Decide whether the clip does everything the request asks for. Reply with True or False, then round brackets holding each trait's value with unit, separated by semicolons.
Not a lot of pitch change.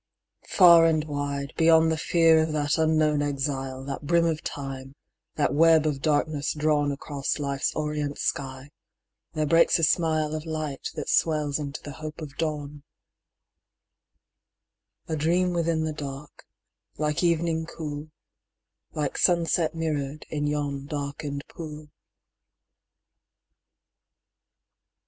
True (2.0 semitones)